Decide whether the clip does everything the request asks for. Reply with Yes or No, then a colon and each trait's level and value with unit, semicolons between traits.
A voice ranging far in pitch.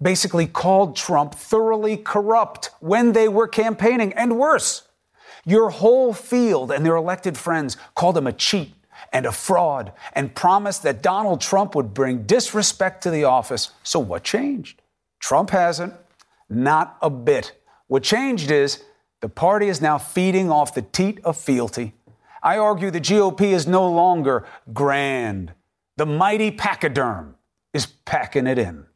Yes: wide, 7.1 semitones